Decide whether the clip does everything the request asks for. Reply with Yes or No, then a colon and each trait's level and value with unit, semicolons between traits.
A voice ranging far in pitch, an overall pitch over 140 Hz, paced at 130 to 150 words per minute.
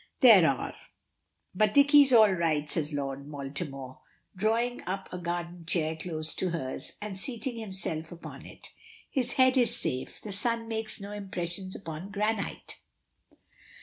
Yes: wide, 5.7 semitones; medium, 185 Hz; average, 145 wpm